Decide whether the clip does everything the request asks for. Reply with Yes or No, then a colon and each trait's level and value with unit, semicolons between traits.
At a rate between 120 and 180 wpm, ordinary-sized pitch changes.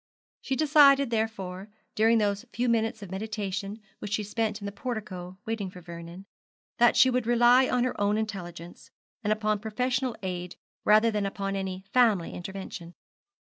Yes: average, 160 wpm; average, 3.4 semitones